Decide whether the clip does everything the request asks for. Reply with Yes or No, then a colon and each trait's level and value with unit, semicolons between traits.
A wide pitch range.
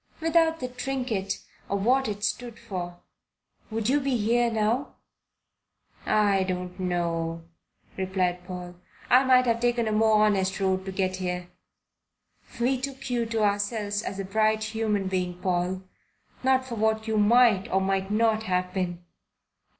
No: average, 4.0 semitones